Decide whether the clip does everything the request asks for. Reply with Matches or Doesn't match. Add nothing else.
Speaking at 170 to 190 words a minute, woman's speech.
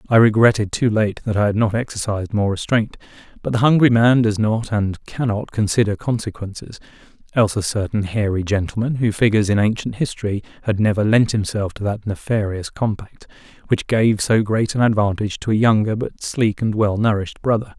Doesn't match